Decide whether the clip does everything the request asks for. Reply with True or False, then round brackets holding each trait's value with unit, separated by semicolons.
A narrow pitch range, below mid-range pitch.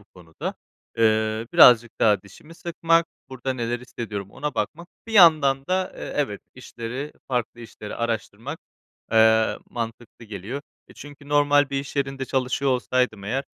False (4.3 semitones; 125 Hz)